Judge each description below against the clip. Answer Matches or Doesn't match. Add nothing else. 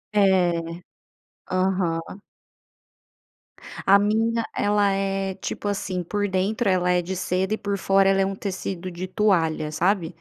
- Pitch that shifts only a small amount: Matches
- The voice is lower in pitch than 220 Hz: Matches